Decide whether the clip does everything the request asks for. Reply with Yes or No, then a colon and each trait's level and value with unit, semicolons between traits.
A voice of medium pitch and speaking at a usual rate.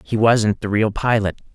No: low, 110 Hz; average, 195 wpm